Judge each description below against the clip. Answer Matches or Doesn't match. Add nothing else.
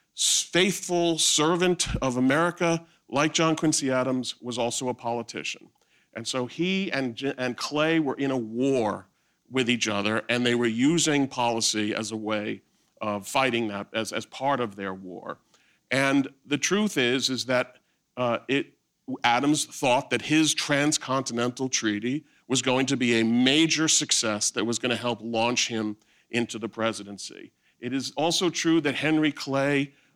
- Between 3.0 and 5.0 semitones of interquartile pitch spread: Matches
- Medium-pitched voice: Doesn't match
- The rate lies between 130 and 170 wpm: Matches